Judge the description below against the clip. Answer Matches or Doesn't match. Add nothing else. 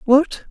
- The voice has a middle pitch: Doesn't match